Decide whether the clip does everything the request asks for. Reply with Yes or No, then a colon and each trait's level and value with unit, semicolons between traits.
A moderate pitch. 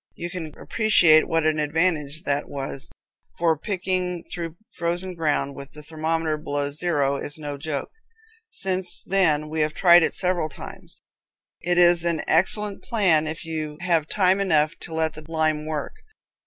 Yes: medium, 160 Hz